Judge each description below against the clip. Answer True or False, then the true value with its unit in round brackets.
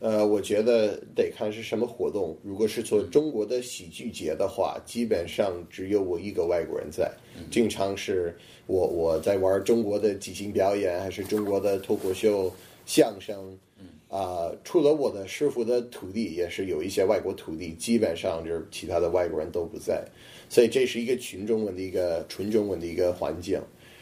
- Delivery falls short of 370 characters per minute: True (280 characters per minute)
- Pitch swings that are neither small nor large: True (4.0 semitones)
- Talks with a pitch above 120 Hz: False (100 Hz)